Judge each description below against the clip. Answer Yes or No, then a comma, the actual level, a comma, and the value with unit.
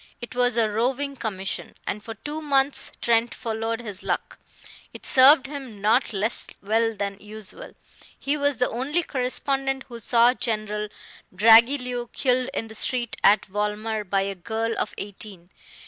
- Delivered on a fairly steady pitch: No, average, 3.4 semitones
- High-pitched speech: Yes, high, 230 Hz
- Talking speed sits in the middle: Yes, average, 155 wpm